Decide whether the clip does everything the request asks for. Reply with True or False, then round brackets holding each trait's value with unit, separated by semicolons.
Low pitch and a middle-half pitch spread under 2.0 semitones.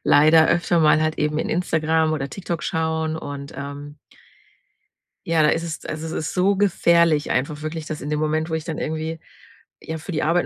False (160 Hz; 1.3 semitones)